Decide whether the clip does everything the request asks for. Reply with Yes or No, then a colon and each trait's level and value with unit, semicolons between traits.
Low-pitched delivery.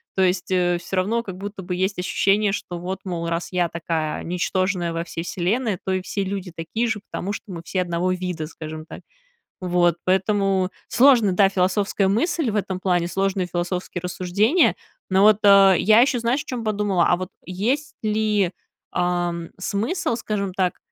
No: high, 190 Hz